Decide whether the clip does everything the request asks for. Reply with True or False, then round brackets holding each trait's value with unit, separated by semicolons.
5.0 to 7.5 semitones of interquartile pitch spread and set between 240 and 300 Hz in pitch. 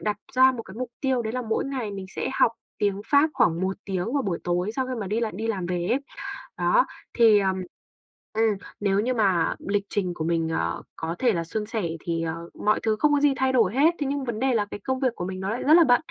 False (5.3 semitones; 215 Hz)